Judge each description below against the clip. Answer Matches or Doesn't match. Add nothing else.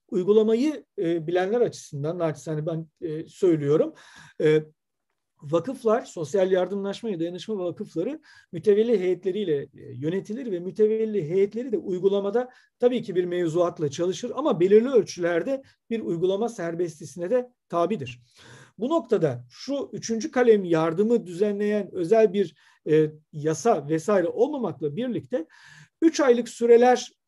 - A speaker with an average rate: Matches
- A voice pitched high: Matches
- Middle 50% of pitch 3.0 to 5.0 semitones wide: Doesn't match